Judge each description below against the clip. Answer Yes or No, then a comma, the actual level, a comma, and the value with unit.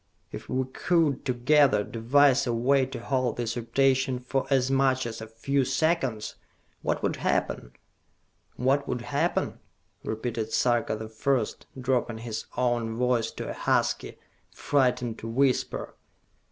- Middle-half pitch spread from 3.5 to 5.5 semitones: No, average, 2.7 semitones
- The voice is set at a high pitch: No, low, 125 Hz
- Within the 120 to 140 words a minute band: Yes, slow, 135 wpm